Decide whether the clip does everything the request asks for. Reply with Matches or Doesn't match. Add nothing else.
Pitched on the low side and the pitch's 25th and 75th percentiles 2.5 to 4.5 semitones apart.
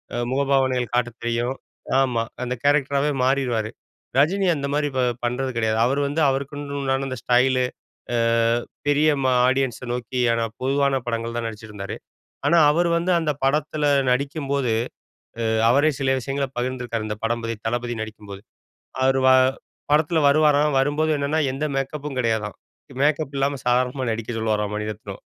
Matches